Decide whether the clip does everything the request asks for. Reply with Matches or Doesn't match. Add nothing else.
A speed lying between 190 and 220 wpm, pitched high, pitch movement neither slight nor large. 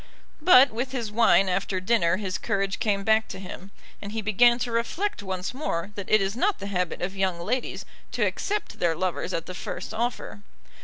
Matches